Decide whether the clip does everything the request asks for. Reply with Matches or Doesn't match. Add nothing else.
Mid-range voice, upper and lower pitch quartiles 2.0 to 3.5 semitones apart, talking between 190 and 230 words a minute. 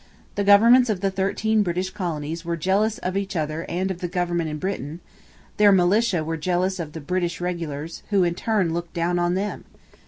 Matches